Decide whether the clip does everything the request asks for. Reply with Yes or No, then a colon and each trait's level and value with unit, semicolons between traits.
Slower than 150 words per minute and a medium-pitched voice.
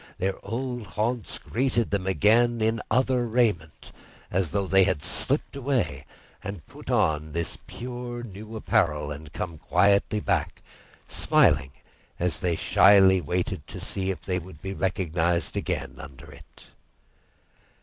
No: average, 140 wpm; very low, 95 Hz